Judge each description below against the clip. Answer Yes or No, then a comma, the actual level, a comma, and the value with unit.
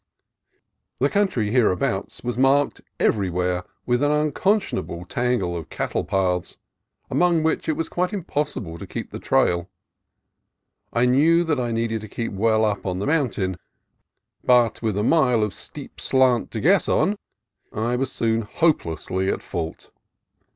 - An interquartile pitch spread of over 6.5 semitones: Yes, wide, 7.0 semitones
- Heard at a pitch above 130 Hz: No, low, 120 Hz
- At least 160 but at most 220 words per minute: No, average, 150 wpm